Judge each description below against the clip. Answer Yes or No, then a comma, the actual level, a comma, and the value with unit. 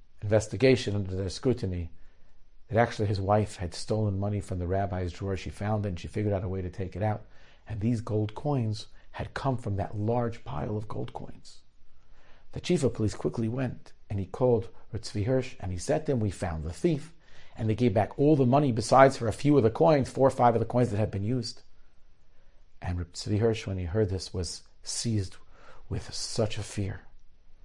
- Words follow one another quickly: Yes, fast, 215 wpm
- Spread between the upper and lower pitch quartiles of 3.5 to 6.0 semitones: Yes, average, 4.2 semitones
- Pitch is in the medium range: No, low, 105 Hz